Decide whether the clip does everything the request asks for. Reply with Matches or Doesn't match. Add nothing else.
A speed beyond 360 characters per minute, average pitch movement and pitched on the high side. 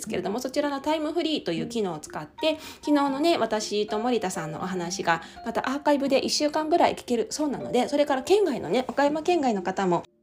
Doesn't match